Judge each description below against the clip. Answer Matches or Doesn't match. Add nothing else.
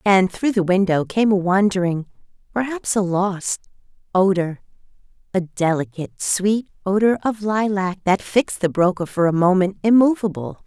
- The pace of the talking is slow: Matches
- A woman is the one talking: Matches